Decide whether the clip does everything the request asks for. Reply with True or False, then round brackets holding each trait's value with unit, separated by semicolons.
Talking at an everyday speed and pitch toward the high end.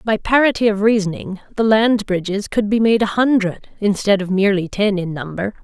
True (190 wpm; 205 Hz)